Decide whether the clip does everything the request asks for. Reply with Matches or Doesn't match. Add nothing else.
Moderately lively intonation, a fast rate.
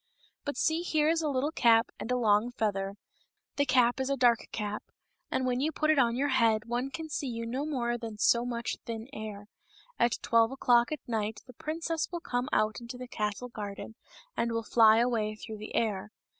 Matches